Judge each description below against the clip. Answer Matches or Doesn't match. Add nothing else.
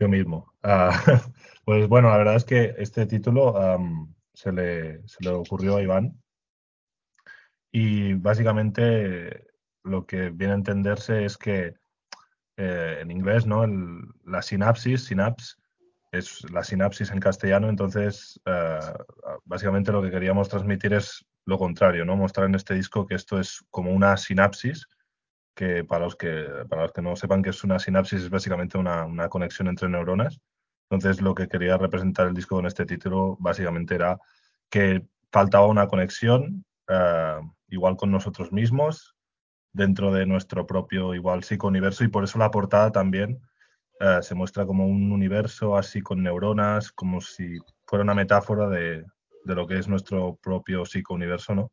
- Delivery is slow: Doesn't match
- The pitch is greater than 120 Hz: Doesn't match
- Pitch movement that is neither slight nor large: Doesn't match